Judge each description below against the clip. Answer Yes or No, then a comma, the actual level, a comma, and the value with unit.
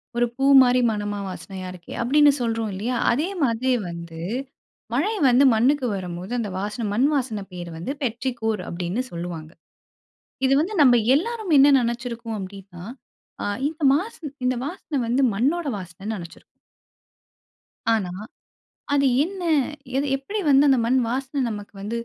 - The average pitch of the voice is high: Yes, high, 235 Hz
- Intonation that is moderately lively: No, wide, 5.7 semitones